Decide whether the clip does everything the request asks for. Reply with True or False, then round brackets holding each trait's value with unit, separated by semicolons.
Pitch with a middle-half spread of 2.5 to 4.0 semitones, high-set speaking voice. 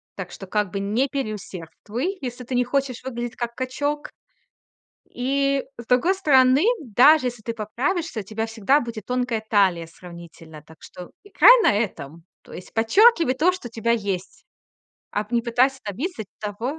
False (4.7 semitones; 235 Hz)